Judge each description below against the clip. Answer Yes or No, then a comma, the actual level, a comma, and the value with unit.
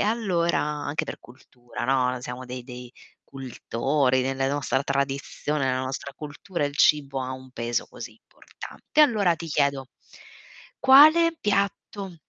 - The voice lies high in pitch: No, medium, 140 Hz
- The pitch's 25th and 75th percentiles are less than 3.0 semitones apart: No, average, 4.7 semitones